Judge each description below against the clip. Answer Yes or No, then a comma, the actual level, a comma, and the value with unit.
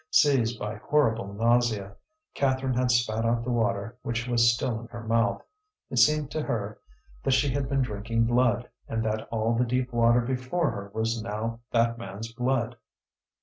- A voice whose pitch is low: Yes, low, 115 Hz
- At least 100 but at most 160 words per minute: No, average, 175 wpm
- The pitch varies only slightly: Yes, narrow, 2.0 semitones